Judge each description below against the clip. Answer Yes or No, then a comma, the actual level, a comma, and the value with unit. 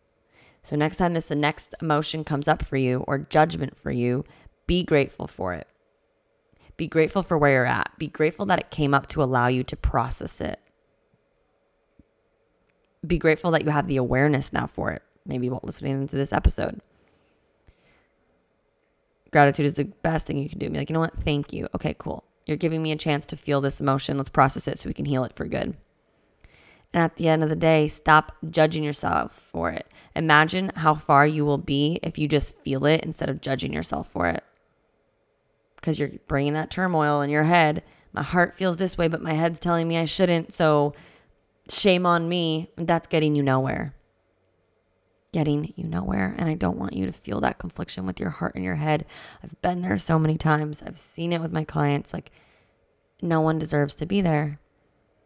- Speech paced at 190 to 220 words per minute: Yes, average, 200 wpm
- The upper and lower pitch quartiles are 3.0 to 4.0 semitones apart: No, narrow, 2.6 semitones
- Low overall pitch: No, medium, 150 Hz